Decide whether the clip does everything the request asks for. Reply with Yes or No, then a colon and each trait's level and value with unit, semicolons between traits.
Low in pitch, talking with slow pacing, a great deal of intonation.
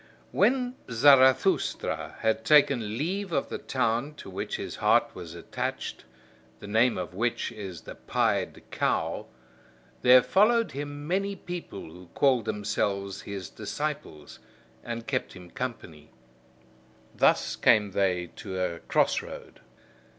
Yes: low, 115 Hz; slow, 125 wpm; wide, 7.0 semitones